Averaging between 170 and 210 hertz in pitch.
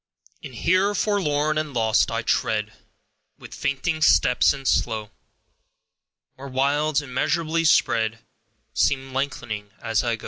No: low, 135 Hz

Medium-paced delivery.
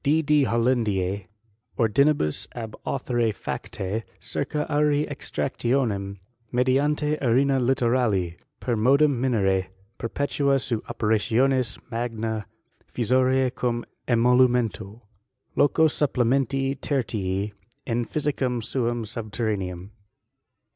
No: slow, 85 wpm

